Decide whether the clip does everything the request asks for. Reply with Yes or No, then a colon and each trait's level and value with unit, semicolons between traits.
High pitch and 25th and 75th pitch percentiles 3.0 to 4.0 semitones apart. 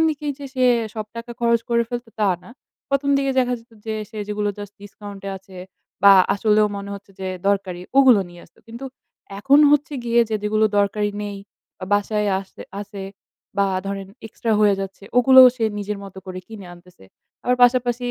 Yes: high, 210 Hz; average, 3.4 semitones